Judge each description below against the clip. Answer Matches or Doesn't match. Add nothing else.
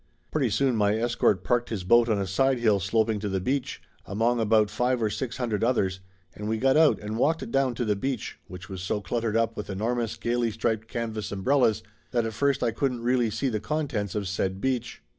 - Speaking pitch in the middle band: Doesn't match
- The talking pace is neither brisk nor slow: Doesn't match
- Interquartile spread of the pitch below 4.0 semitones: Matches